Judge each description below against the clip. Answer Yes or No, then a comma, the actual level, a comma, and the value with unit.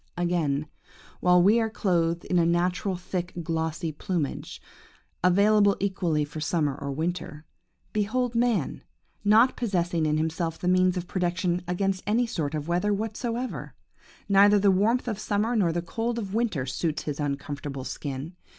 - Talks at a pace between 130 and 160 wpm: Yes, average, 150 wpm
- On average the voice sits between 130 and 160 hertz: No, medium, 180 Hz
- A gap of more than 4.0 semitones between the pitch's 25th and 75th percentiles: Yes, average, 4.4 semitones